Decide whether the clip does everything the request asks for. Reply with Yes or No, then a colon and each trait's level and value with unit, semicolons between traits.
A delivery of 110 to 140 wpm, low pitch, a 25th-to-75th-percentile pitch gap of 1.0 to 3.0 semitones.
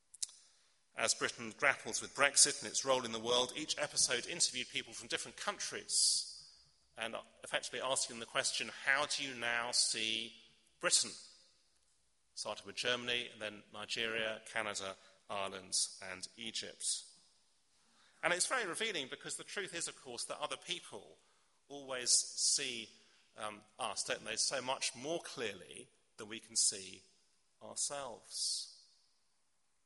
No: slow, 135 wpm; low, 120 Hz; average, 3.6 semitones